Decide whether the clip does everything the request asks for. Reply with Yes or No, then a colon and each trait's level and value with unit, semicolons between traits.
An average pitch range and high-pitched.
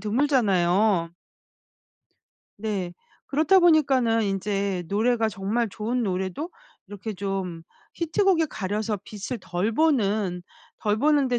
Yes: average, 4.7 semitones; high, 215 Hz